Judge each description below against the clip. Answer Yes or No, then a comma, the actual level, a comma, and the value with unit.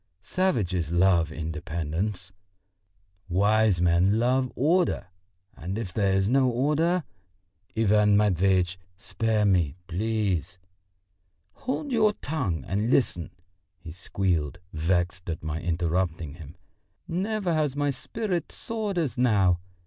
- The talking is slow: Yes, slow, 110 wpm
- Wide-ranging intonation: Yes, wide, 7.2 semitones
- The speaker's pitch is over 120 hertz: No, low, 100 Hz